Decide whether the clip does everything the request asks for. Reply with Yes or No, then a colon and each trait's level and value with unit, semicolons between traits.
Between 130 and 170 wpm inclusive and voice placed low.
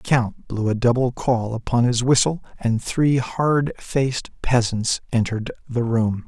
Yes: average, 165 wpm; low, 120 Hz